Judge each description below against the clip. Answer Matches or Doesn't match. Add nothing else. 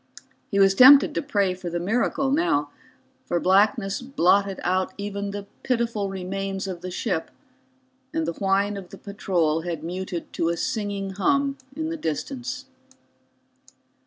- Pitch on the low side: Doesn't match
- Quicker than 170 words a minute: Doesn't match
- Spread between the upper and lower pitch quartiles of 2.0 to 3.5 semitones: Doesn't match